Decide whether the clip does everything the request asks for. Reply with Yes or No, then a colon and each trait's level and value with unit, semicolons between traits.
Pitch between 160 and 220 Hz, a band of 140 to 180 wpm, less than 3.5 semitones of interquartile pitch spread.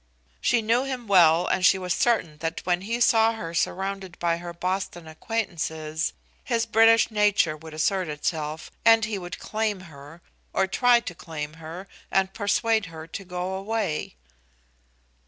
No: medium, 185 Hz; average, 155 wpm; average, 5.1 semitones